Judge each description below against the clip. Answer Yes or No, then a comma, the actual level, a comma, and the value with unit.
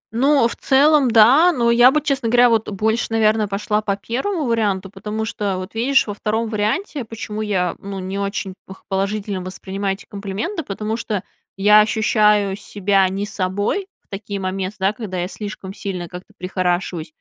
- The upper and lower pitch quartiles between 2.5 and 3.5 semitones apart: Yes, average, 2.9 semitones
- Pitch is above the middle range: Yes, high, 210 Hz